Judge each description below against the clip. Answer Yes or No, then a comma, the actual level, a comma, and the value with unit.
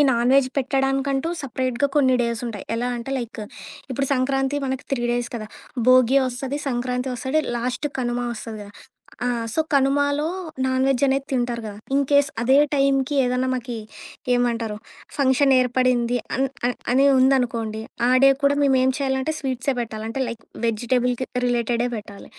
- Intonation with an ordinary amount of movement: No, narrow, 2.1 semitones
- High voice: Yes, very high, 255 Hz